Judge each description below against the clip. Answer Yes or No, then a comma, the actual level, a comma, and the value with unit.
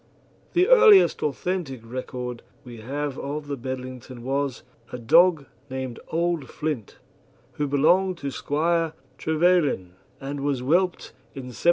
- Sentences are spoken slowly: Yes, slow, 130 wpm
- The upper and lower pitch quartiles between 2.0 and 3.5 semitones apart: No, average, 4.6 semitones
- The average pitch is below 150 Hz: Yes, medium, 140 Hz